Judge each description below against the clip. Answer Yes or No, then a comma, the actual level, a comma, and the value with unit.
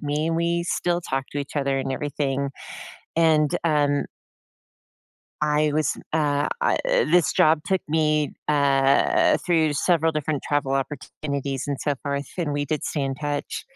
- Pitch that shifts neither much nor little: No, narrow, 2.1 semitones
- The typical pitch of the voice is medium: Yes, medium, 150 Hz